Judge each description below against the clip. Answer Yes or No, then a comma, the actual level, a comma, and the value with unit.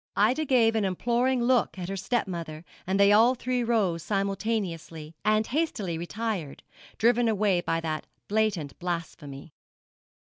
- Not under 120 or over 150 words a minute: Yes, slow, 135 wpm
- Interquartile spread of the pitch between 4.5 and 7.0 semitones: Yes, average, 5.2 semitones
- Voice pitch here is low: No, high, 200 Hz